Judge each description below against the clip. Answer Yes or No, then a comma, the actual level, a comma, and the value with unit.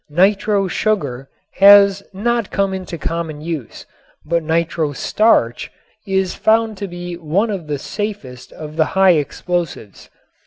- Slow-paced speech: Yes, slow, 125 wpm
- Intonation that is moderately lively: Yes, average, 4.2 semitones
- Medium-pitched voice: Yes, medium, 175 Hz